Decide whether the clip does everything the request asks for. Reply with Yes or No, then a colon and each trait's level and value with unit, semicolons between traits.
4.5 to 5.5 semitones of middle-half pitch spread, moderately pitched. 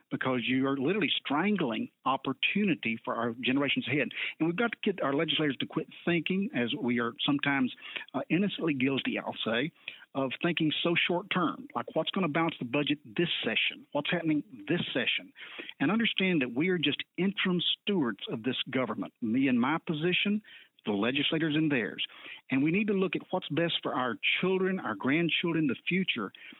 Yes: average, 5.0 semitones; medium, 165 Hz